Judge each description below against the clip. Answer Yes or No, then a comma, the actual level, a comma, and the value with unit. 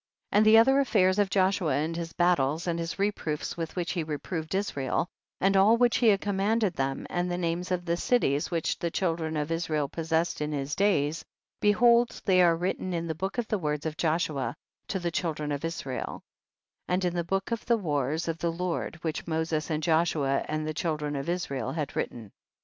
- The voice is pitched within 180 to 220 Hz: No, medium, 170 Hz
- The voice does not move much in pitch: No, average, 3.7 semitones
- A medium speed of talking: No, fast, 210 wpm